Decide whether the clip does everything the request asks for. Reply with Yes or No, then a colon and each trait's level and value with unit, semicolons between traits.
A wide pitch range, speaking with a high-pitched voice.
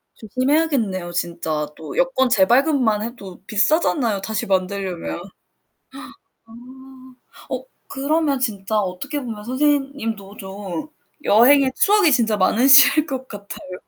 Yes: wide, 6.0 semitones; high, 225 Hz